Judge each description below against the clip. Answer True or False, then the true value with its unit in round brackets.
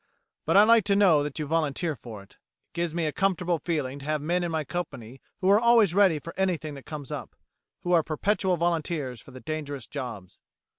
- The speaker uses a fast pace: True (215 wpm)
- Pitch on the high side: False (160 Hz)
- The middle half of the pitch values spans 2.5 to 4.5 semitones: True (3.9 semitones)